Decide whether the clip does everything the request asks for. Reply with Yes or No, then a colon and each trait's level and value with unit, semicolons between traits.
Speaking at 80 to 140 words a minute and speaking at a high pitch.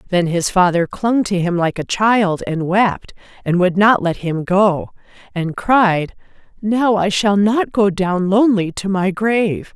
No: average, 180 wpm; high, 195 Hz